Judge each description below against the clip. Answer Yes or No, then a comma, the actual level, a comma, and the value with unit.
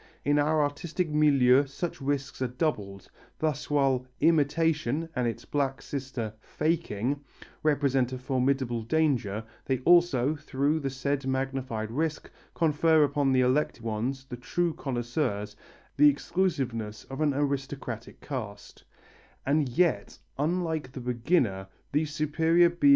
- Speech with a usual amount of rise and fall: Yes, average, 3.2 semitones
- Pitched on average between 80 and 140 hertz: Yes, low, 135 Hz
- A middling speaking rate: No, slow, 105 wpm